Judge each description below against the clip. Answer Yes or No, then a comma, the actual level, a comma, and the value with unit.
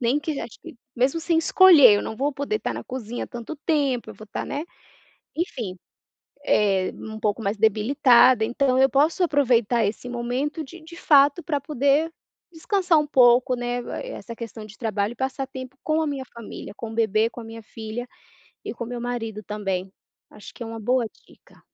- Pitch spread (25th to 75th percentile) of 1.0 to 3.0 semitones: No, average, 4.2 semitones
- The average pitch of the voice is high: Yes, high, 245 Hz